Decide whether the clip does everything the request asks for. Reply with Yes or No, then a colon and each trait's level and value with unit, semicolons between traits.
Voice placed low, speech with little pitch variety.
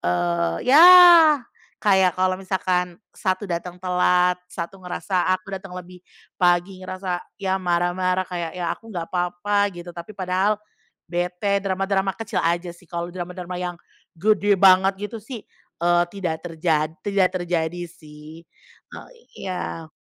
No: medium, 180 Hz; narrow, 1.7 semitones